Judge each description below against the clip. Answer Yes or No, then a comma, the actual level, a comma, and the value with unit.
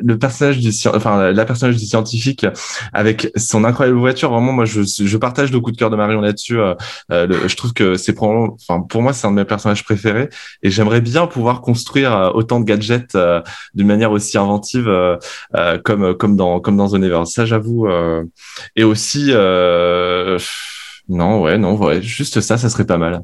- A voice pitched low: Yes, low, 110 Hz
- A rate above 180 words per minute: Yes, average, 200 wpm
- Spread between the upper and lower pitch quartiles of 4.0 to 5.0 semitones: No, average, 3.1 semitones